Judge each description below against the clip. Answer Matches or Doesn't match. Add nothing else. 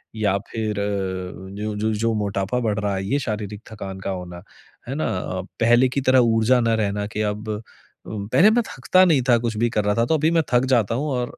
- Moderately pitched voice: Doesn't match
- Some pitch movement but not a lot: Matches